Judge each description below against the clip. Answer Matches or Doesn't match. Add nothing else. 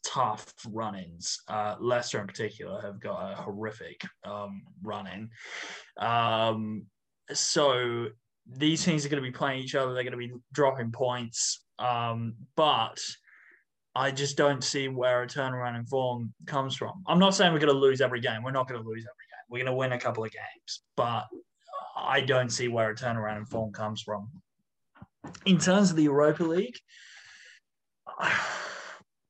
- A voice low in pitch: Matches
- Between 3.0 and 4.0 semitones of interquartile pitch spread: Matches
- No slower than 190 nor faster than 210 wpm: Doesn't match